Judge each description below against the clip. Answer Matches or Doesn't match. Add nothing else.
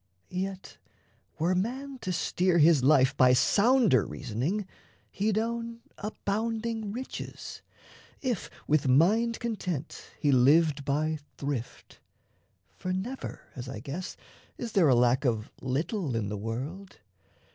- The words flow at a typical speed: Doesn't match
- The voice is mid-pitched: Matches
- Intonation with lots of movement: Matches